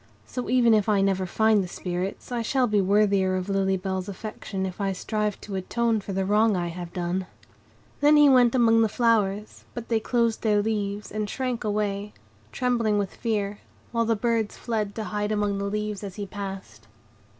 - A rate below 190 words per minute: No, average, 195 wpm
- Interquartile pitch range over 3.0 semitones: No, average, 2.7 semitones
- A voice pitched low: No, high, 210 Hz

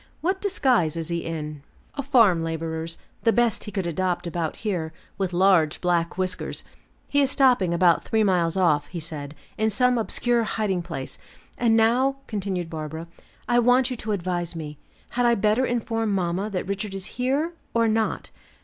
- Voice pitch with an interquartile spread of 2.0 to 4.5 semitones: No, wide, 5.6 semitones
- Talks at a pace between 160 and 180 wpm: Yes, average, 175 wpm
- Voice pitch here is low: No, high, 190 Hz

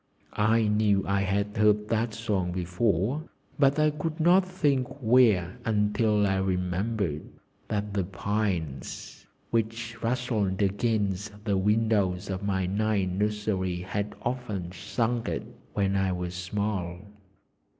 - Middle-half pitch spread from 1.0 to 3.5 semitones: Yes, average, 3.2 semitones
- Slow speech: Yes, slow, 125 wpm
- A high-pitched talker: No, low, 105 Hz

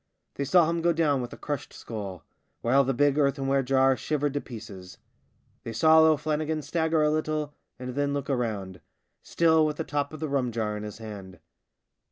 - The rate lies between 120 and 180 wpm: No, average, 195 wpm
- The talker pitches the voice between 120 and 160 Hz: Yes, medium, 140 Hz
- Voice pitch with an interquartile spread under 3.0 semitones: No, average, 4.7 semitones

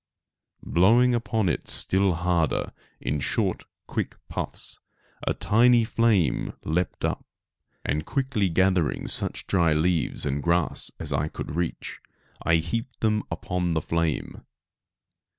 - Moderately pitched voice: No, very low, 90 Hz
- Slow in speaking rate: Yes, slow, 125 wpm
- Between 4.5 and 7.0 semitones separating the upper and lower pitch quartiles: Yes, average, 5.2 semitones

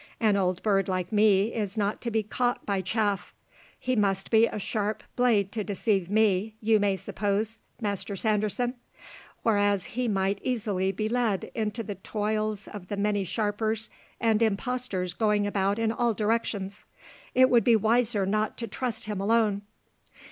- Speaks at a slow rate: No, average, 160 wpm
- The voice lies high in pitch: Yes, high, 210 Hz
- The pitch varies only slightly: Yes, narrow, 2.1 semitones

